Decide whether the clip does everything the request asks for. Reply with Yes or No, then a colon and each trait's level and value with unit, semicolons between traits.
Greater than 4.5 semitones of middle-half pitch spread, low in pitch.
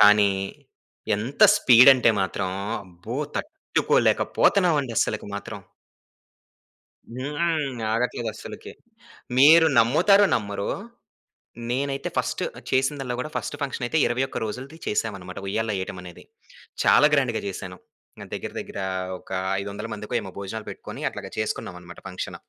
Yes: wide, 5.4 semitones; low, 120 Hz